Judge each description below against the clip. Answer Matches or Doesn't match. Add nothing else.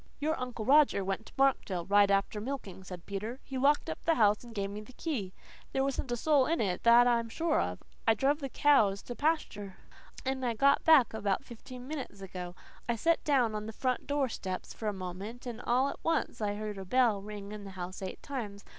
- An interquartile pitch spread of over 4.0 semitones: Matches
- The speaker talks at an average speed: Doesn't match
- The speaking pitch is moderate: Doesn't match